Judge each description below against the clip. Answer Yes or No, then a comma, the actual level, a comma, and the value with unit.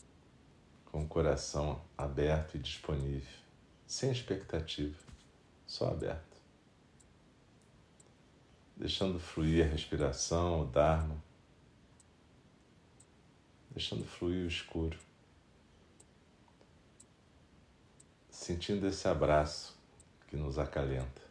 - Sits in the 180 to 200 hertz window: No, very low, 80 Hz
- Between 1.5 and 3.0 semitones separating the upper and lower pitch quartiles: Yes, average, 2.7 semitones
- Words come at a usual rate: No, slow, 75 wpm